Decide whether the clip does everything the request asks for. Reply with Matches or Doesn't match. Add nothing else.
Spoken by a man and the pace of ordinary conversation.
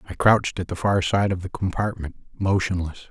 Matches